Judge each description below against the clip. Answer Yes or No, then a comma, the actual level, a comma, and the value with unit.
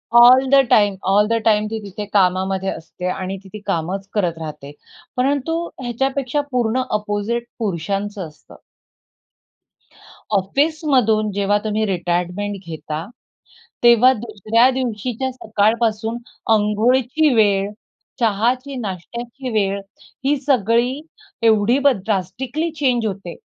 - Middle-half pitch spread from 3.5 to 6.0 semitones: Yes, average, 4.2 semitones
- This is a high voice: Yes, high, 215 Hz